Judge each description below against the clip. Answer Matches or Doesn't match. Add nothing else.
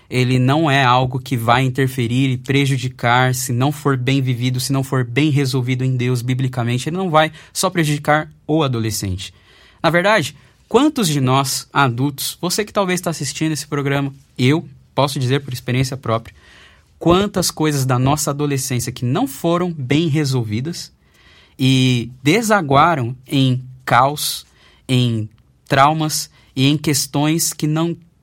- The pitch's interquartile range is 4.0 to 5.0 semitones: Doesn't match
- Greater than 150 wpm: Doesn't match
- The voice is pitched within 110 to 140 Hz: Matches